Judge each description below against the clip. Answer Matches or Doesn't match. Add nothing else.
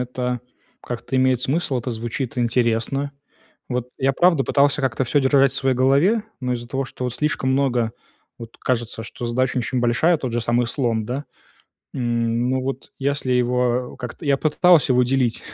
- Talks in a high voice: Doesn't match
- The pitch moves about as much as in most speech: Doesn't match